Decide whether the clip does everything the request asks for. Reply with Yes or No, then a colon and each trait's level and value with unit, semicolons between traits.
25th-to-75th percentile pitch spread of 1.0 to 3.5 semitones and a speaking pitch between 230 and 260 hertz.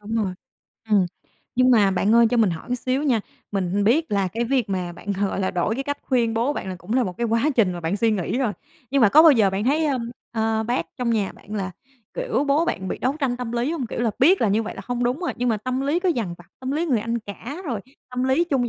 No: average, 4.5 semitones; high, 235 Hz